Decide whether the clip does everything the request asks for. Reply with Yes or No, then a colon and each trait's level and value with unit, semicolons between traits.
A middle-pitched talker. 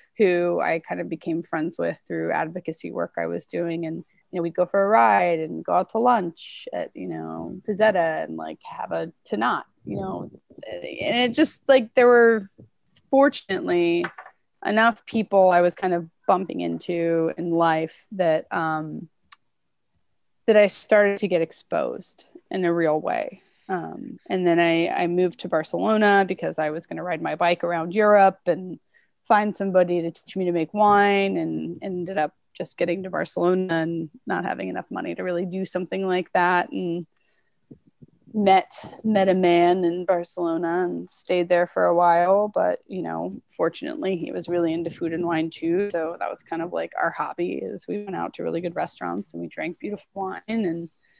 Yes: medium, 175 Hz